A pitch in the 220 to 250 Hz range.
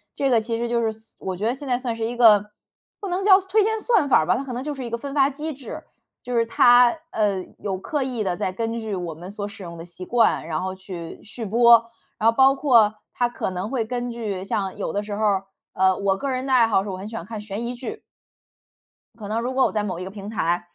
Yes: high, 225 Hz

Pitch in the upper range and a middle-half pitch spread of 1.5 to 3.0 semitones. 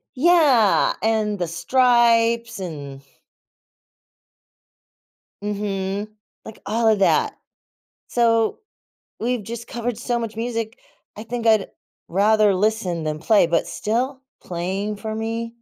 Yes: high, 220 Hz; average, 2.7 semitones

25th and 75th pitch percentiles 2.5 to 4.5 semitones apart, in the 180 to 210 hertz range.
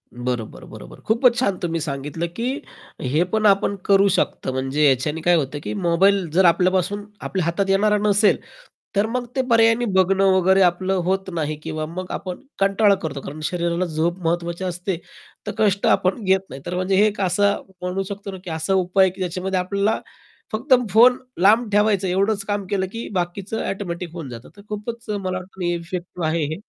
Yes: average, 3.0 semitones; medium, 185 Hz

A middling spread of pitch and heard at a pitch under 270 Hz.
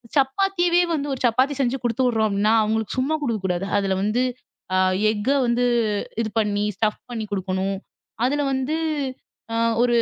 Yes: average, 4.3 semitones; high, 235 Hz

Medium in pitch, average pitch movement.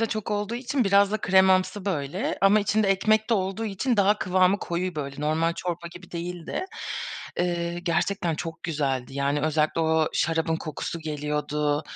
Yes: medium, 175 Hz; average, 4.1 semitones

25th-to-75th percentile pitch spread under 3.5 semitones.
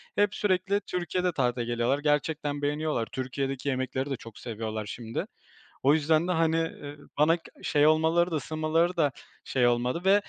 No: average, 4.2 semitones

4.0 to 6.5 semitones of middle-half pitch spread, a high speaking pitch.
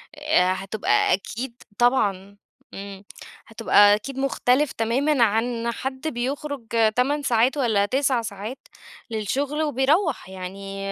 Yes: average, 5.1 semitones; high, 235 Hz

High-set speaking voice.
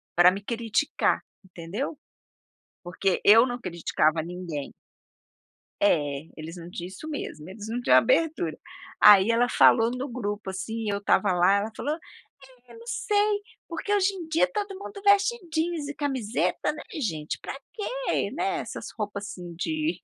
Yes: high, 225 Hz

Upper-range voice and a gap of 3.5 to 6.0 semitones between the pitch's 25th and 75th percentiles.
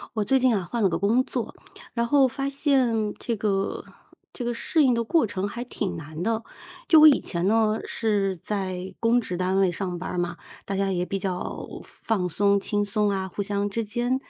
Yes: high, 205 Hz; average, 3.8 semitones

